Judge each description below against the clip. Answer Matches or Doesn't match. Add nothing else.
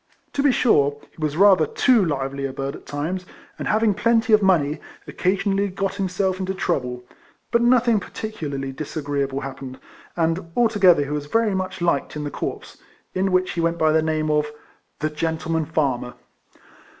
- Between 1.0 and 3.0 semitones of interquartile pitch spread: Doesn't match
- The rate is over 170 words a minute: Matches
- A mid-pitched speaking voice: Matches